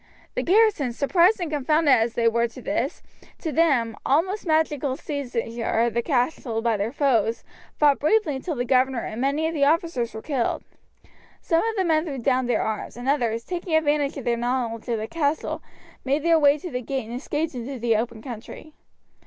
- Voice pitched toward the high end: Yes, very high, 270 Hz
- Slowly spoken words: No, average, 195 wpm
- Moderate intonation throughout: Yes, average, 4.9 semitones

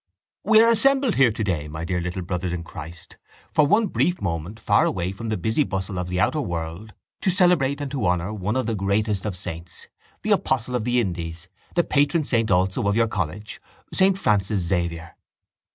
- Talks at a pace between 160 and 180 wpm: No, average, 195 wpm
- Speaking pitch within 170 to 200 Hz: No, low, 100 Hz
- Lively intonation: Yes, wide, 7.0 semitones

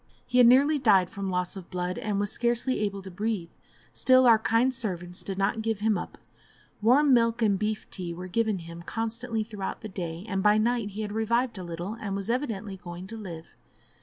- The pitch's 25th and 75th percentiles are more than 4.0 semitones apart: No, average, 3.6 semitones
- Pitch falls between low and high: No, high, 210 Hz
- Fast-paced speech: Yes, fast, 210 wpm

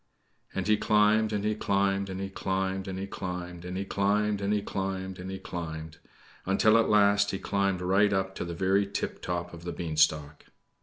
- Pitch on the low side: Yes, very low, 95 Hz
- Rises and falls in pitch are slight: Yes, narrow, 2.1 semitones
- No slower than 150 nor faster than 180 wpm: No, average, 195 wpm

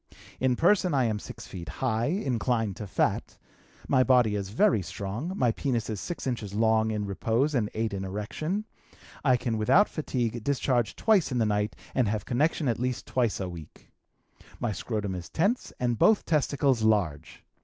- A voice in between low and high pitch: No, low, 115 Hz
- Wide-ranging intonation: No, average, 4.2 semitones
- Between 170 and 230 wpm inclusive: Yes, average, 175 wpm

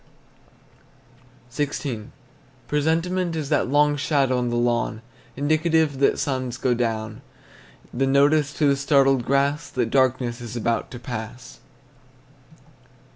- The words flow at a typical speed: No, slow, 120 wpm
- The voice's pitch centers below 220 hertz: Yes, low, 135 Hz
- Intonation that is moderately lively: Yes, average, 3.4 semitones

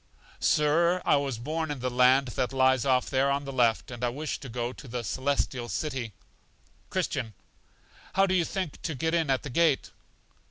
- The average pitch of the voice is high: No, low, 135 Hz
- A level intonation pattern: No, average, 3.4 semitones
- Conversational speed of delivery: Yes, average, 195 wpm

